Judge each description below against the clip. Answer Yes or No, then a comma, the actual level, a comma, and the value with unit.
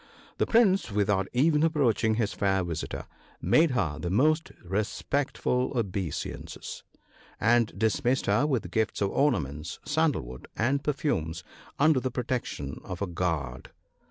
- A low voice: Yes, low, 110 Hz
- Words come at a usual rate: No, slow, 130 wpm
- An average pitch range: No, wide, 7.8 semitones